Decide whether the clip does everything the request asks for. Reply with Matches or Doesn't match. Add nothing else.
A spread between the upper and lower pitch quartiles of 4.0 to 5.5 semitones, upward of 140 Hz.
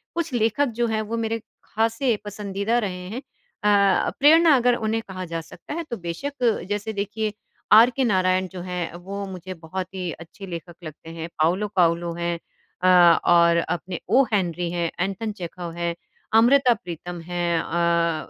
Matches